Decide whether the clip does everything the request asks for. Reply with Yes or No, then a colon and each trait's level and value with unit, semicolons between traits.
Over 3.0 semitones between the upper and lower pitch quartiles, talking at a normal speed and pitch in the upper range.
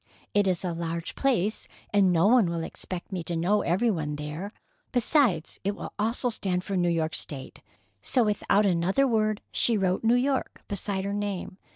Yes: average, 3.9 semitones; average, 185 wpm; high, 195 Hz